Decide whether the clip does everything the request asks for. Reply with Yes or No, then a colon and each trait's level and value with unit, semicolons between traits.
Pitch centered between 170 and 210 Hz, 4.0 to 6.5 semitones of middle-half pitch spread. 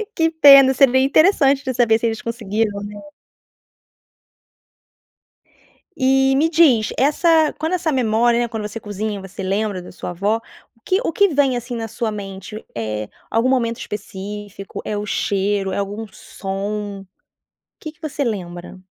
No: high, 225 Hz; average, 4.9 semitones